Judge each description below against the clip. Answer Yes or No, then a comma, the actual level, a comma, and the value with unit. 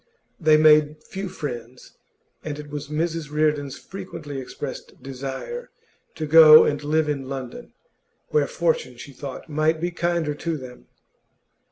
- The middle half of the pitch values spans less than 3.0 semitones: Yes, narrow, 2.5 semitones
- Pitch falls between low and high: Yes, medium, 150 Hz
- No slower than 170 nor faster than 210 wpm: No, average, 140 wpm